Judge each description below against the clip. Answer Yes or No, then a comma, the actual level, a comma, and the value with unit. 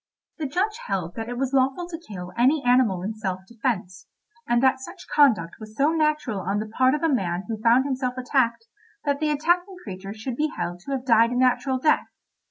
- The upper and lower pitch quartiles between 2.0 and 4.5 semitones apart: No, average, 5.0 semitones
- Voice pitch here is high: Yes, very high, 250 Hz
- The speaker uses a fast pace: Yes, fast, 210 wpm